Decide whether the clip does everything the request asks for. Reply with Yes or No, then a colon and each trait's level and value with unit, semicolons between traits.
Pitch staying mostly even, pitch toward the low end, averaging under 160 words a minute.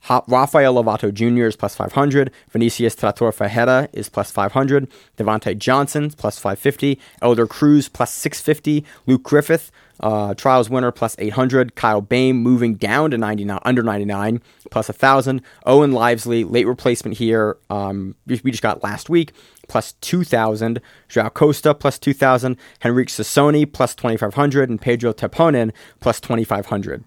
No: average, 3.6 semitones; low, 120 Hz; average, 140 wpm